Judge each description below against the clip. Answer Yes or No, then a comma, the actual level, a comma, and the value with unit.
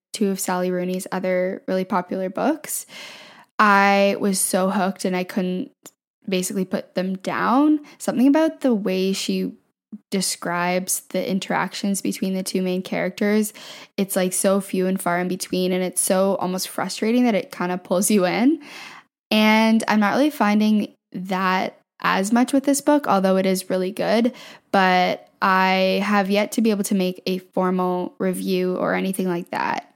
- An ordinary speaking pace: Yes, average, 170 wpm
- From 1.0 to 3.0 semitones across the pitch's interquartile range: Yes, narrow, 2.5 semitones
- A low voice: No, high, 190 Hz